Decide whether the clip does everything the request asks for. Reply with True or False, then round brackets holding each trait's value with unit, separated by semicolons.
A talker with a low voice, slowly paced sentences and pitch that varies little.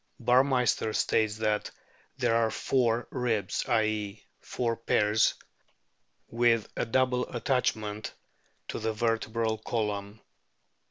True (115 Hz; 100 wpm; 1.9 semitones)